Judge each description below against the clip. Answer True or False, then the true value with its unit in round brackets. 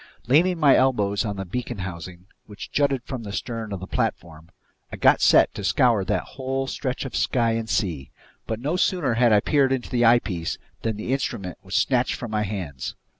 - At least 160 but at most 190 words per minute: False (200 wpm)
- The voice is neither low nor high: False (115 Hz)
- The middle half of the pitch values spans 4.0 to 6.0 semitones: True (5.1 semitones)